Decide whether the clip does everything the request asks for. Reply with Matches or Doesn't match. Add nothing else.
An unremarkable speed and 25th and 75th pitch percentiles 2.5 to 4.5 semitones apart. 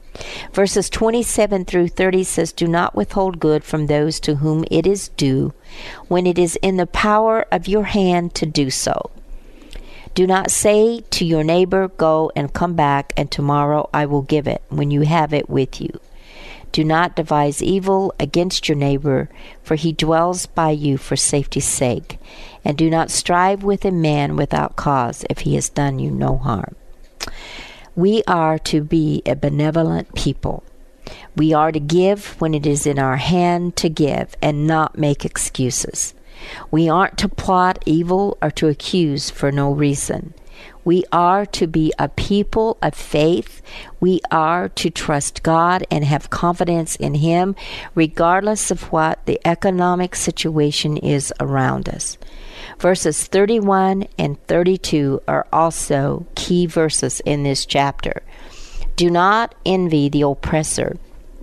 Matches